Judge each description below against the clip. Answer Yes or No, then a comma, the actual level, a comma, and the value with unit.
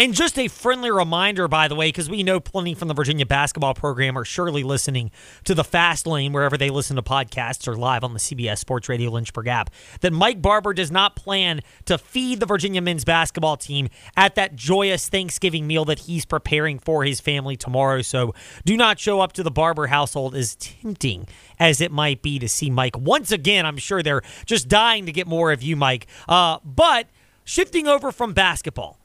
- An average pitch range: No, wide, 5.9 semitones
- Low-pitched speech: No, medium, 155 Hz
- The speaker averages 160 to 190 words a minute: No, fast, 205 wpm